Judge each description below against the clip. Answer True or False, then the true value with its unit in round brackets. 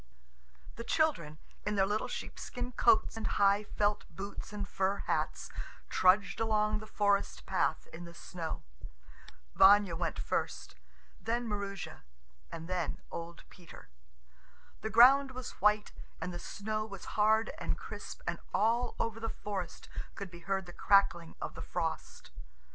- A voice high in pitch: True (205 Hz)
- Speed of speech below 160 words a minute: True (145 wpm)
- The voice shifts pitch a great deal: False (3.2 semitones)